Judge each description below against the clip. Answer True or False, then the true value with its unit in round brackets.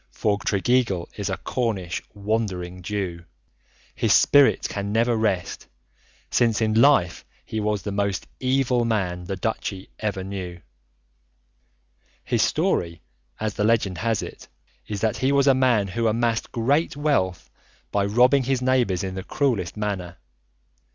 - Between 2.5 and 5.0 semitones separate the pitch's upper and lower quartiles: True (4.1 semitones)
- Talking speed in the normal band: True (145 wpm)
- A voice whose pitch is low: True (105 Hz)